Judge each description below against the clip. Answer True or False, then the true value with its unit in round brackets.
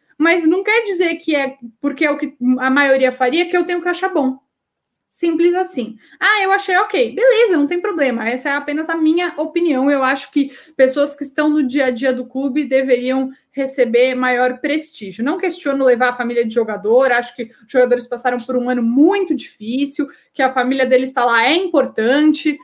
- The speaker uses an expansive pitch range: False (4.5 semitones)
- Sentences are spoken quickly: True (200 wpm)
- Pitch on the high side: True (280 Hz)